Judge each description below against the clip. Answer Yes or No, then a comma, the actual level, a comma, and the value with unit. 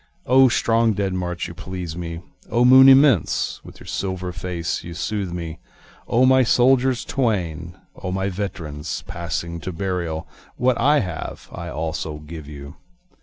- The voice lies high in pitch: No, very low, 90 Hz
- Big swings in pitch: Yes, wide, 5.8 semitones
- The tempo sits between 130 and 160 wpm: Yes, average, 155 wpm